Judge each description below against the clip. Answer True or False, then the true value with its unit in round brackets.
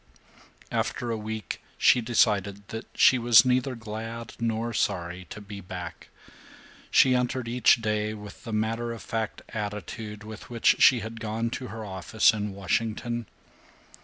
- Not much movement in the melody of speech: True (2.0 semitones)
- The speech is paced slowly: False (150 wpm)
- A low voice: True (110 Hz)